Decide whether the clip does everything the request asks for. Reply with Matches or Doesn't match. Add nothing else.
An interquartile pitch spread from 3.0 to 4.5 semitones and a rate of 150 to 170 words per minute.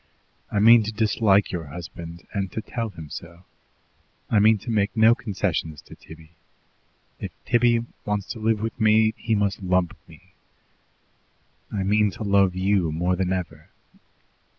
Matches